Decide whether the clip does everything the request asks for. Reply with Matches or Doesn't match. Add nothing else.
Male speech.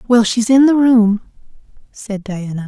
Doesn't match